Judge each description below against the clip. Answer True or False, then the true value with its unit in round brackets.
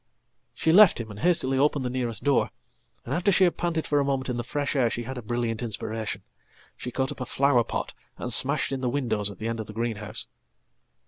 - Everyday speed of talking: False (215 wpm)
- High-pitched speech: False (130 Hz)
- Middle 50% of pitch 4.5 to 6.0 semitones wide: False (3.7 semitones)